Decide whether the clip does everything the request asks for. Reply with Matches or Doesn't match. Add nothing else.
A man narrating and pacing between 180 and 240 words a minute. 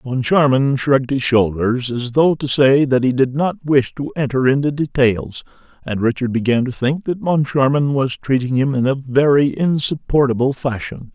Doesn't match